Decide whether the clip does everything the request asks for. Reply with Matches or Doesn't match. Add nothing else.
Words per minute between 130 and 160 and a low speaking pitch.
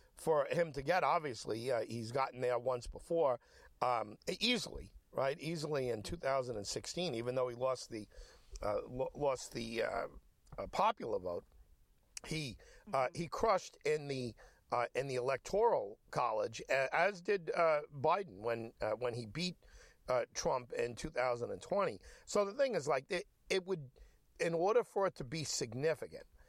Doesn't match